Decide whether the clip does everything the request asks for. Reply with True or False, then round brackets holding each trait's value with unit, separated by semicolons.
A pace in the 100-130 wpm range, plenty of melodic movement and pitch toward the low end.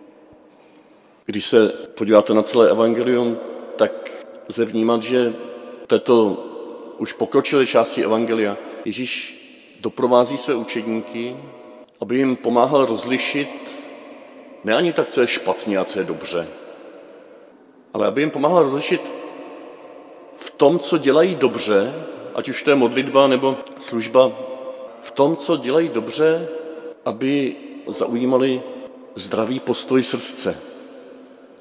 True (115 wpm; 5.9 semitones; 130 Hz)